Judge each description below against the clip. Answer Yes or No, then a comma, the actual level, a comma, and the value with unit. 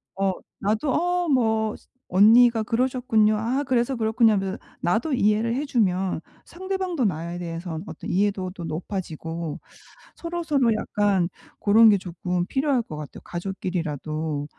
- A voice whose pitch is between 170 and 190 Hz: No, high, 210 Hz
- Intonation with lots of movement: Yes, wide, 5.7 semitones